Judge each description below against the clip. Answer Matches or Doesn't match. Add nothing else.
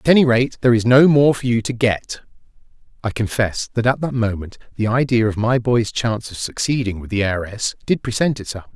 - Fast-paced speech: Matches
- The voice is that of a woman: Doesn't match